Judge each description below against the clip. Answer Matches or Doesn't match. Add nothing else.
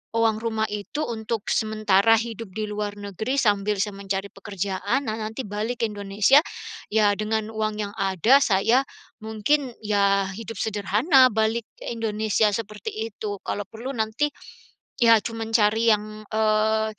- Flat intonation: Matches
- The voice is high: Matches